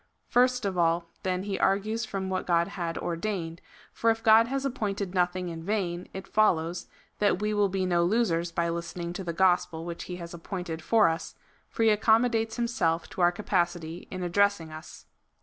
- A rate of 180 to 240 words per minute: Yes, average, 185 wpm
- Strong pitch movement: No, average, 3.7 semitones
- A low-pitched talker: No, medium, 185 Hz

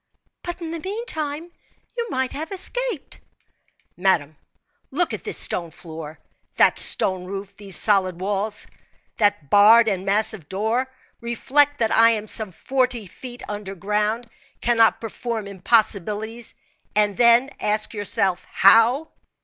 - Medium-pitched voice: No, high, 220 Hz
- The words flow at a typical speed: No, slow, 130 wpm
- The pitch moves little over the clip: No, average, 4.1 semitones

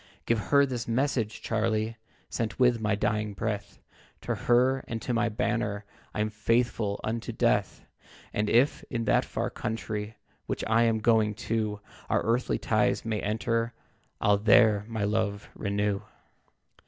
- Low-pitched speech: Yes, low, 110 Hz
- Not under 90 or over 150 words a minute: Yes, average, 145 wpm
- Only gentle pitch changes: Yes, narrow, 1.8 semitones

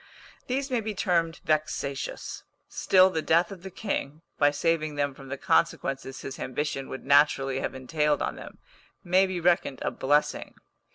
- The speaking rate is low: No, average, 165 wpm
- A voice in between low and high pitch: Yes, medium, 150 Hz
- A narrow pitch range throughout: No, average, 4.5 semitones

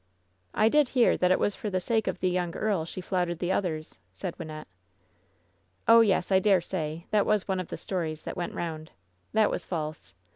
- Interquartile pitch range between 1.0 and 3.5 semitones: No, average, 3.9 semitones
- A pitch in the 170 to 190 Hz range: Yes, medium, 185 Hz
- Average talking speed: No, fast, 215 wpm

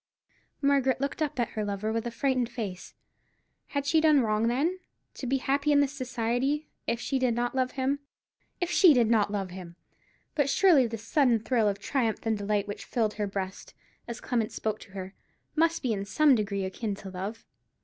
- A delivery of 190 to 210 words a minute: Yes, average, 195 wpm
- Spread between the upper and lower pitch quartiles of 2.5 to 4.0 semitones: No, average, 4.8 semitones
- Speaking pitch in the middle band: No, high, 235 Hz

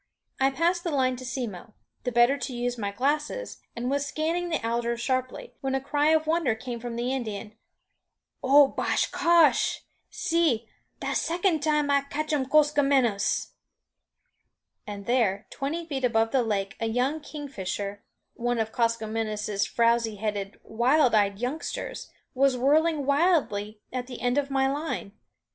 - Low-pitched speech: No, very high, 255 Hz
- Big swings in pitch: No, average, 4.5 semitones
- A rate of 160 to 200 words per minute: No, average, 150 wpm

